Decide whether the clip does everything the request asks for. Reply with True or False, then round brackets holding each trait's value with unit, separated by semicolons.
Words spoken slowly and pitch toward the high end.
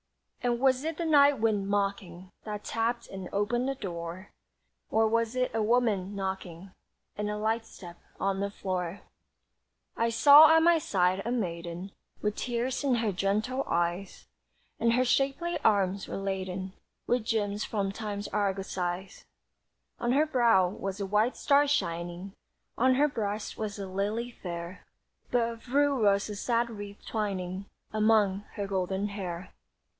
False (155 wpm; 205 Hz)